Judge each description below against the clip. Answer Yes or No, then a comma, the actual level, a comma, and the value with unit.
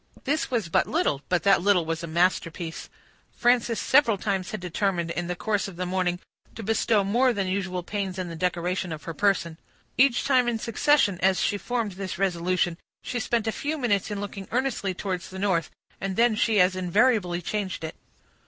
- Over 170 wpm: Yes, average, 195 wpm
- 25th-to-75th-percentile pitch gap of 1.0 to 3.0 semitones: No, average, 3.9 semitones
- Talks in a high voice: Yes, high, 195 Hz